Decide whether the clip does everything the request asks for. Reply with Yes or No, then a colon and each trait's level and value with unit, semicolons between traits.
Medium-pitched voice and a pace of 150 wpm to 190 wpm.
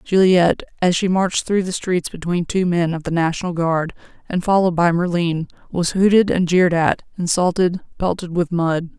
Yes: medium, 175 Hz; average, 180 wpm